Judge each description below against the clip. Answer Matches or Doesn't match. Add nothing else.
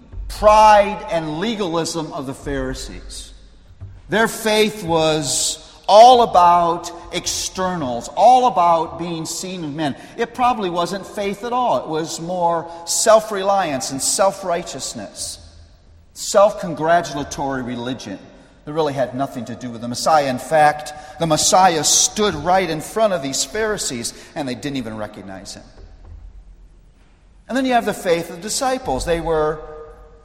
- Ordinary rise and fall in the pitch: Doesn't match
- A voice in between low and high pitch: Matches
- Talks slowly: Doesn't match